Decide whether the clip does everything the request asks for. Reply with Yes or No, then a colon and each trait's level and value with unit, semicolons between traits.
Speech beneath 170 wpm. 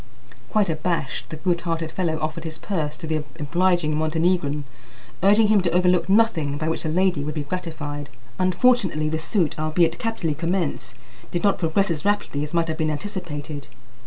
No: average, 175 wpm